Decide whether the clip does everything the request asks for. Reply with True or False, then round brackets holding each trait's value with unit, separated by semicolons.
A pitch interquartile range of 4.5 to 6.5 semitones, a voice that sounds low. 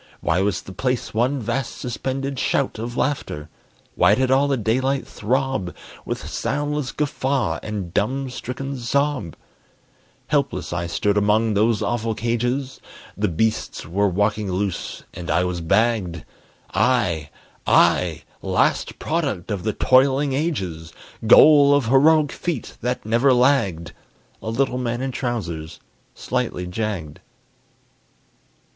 True (5.3 semitones; 115 Hz)